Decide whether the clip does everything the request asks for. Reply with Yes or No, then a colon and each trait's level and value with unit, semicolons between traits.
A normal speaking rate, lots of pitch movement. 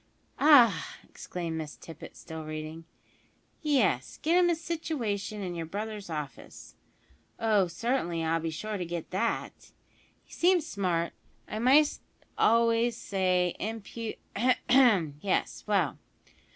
No: slow, 125 wpm; wide, 6.2 semitones